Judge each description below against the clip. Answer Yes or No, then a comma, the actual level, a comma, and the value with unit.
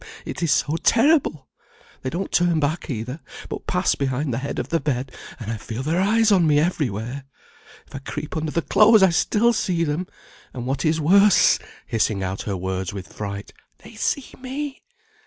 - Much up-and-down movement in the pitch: Yes, wide, 6.9 semitones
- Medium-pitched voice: Yes, medium, 150 Hz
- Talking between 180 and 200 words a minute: Yes, average, 190 wpm